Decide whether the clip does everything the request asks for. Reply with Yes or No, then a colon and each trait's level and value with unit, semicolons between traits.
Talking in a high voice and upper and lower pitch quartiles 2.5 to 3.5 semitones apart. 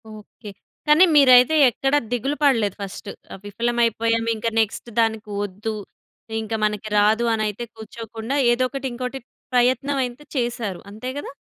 Yes: high, 230 Hz; average, 2.8 semitones